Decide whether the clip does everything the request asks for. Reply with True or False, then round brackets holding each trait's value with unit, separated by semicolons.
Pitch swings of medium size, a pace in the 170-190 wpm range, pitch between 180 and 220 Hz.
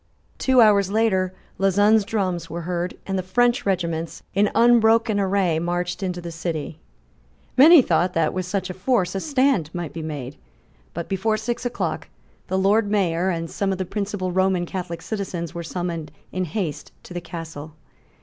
True (3.3 semitones; 175 wpm; 185 Hz)